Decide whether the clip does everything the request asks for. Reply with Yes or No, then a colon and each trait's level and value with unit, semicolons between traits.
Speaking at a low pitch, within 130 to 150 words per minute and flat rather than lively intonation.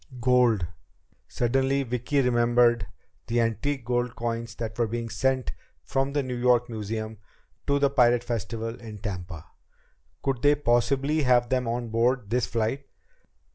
Yes: low, 120 Hz; average, 140 wpm; narrow, 2.2 semitones